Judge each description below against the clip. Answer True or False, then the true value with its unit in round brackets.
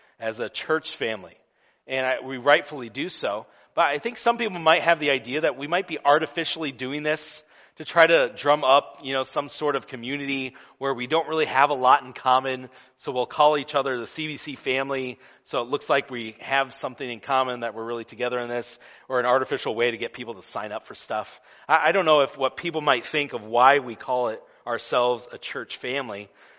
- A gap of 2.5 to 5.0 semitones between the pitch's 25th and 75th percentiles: True (3.5 semitones)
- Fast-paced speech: True (225 wpm)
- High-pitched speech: False (135 Hz)